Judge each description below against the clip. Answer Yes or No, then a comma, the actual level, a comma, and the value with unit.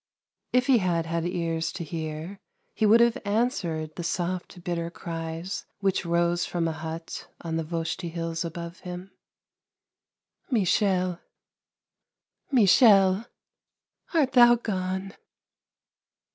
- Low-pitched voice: No, medium, 175 Hz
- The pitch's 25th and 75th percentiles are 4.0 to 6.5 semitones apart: No, average, 3.2 semitones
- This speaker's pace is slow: Yes, slow, 115 wpm